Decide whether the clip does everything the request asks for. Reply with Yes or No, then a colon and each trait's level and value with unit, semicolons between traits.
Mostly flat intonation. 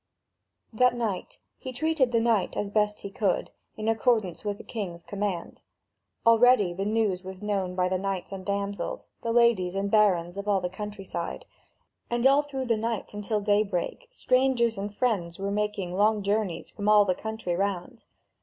No: average, 3.0 semitones